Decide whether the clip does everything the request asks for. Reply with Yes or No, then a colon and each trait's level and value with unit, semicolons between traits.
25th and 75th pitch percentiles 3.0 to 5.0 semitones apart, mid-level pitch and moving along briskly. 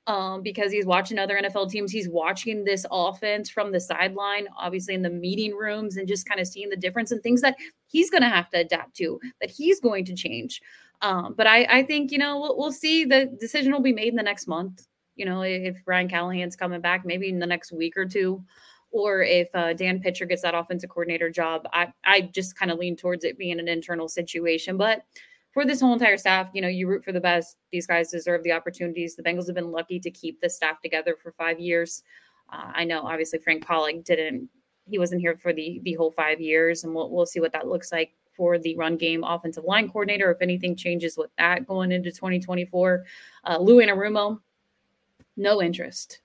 Yes: average, 3.3 semitones; medium, 180 Hz; fast, 220 wpm